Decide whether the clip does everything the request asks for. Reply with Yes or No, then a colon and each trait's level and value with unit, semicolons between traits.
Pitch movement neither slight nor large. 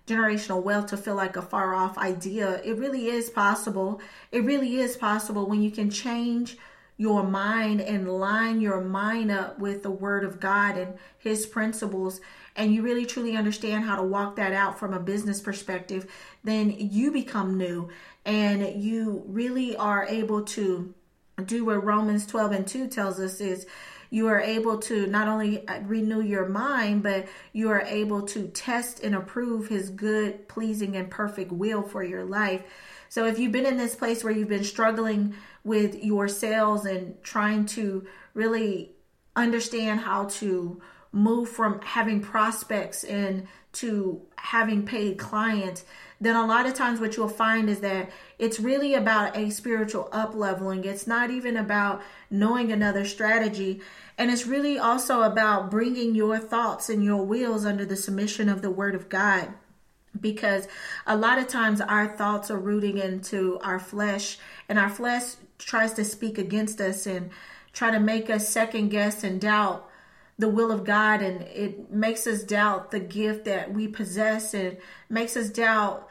No: narrow, 2.1 semitones